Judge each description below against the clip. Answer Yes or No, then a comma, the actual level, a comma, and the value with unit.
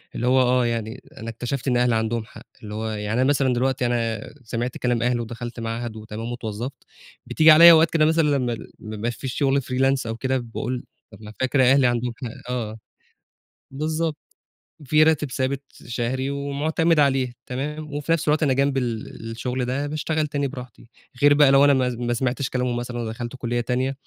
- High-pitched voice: No, low, 125 Hz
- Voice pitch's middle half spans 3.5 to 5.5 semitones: No, average, 3.0 semitones